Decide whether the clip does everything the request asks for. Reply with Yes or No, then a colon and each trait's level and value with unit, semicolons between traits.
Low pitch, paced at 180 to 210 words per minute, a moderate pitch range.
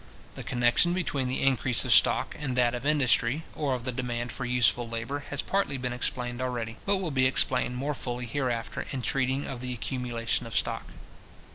No: low, 125 Hz; average, 190 wpm; narrow, 2.1 semitones